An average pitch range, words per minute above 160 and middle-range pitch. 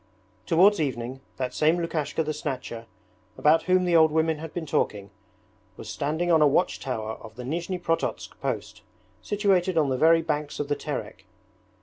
Yes: average, 3.8 semitones; average, 175 wpm; medium, 155 Hz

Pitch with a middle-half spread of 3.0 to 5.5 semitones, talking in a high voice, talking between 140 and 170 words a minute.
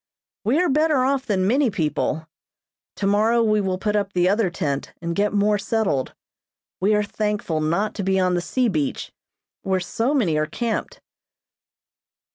Yes: average, 3.9 semitones; high, 205 Hz; average, 165 wpm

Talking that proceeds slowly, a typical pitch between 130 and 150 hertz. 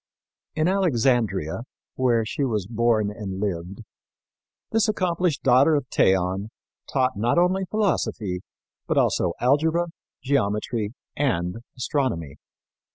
No: slow, 105 wpm; low, 120 Hz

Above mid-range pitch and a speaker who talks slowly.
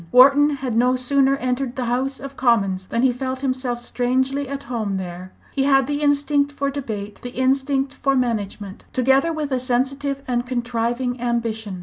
No: very high, 255 Hz; average, 175 wpm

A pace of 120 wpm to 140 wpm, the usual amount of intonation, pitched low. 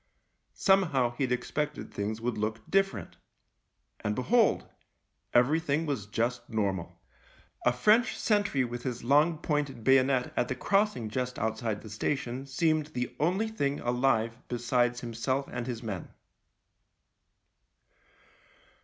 Yes: slow, 135 wpm; average, 4.3 semitones; low, 125 Hz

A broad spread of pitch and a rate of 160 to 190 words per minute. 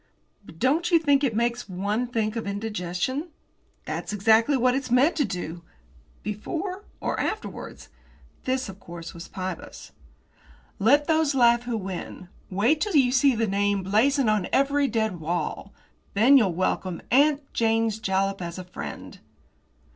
No: wide, 5.8 semitones; average, 150 wpm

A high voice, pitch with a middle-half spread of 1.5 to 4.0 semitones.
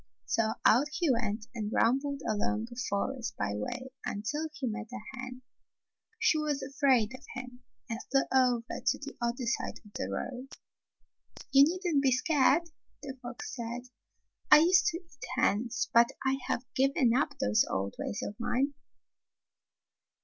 Yes: very high, 255 Hz; average, 3.3 semitones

